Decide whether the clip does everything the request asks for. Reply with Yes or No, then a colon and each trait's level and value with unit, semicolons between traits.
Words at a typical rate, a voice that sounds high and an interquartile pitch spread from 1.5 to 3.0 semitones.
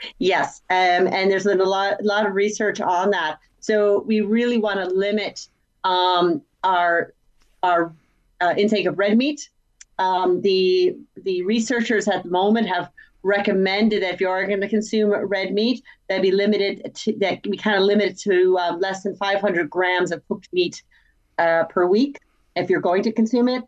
Yes: average, 190 wpm; high, 200 Hz; narrow, 2.6 semitones